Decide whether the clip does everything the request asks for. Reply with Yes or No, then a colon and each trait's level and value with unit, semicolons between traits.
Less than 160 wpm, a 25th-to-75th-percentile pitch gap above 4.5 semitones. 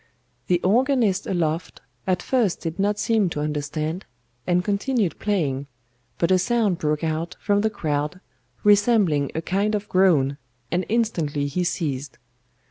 Yes: average, 140 wpm; average, 5.2 semitones